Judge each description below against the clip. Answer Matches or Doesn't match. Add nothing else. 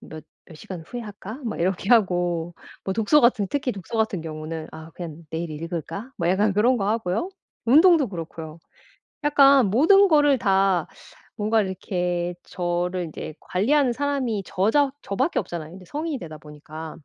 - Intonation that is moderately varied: Doesn't match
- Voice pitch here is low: Doesn't match